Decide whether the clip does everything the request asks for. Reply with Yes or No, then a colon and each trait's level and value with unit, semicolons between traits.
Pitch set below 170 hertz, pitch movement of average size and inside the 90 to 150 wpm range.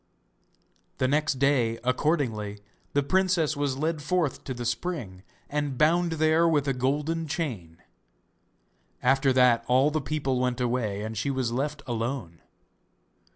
Yes: low, 135 Hz; average, 4.0 semitones; average, 140 wpm